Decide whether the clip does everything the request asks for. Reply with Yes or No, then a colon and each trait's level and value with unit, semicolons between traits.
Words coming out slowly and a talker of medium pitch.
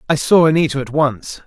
No: fast, 205 wpm; medium, 145 Hz